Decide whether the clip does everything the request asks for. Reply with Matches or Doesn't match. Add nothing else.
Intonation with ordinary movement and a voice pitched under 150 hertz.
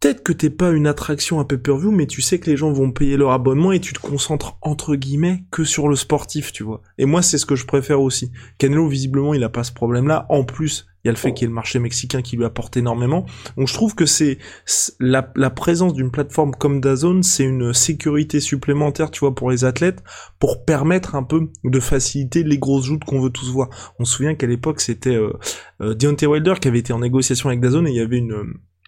Matches